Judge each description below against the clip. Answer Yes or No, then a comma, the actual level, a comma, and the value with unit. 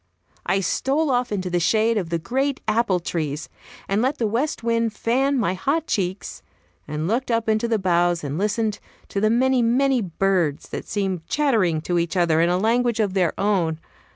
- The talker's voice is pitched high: Yes, high, 210 Hz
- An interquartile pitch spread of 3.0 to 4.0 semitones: No, average, 5.2 semitones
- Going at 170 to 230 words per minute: Yes, average, 190 wpm